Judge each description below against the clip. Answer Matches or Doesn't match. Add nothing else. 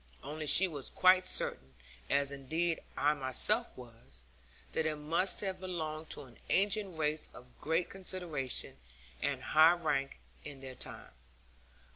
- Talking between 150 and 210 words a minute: Doesn't match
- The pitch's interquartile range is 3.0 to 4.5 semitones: Doesn't match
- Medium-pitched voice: Matches